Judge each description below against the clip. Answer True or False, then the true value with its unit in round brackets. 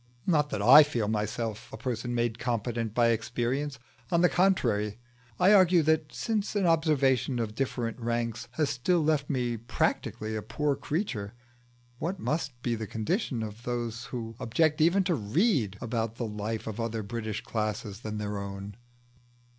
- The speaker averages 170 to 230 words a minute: False (160 wpm)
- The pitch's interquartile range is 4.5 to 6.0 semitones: True (5.2 semitones)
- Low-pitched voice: True (120 Hz)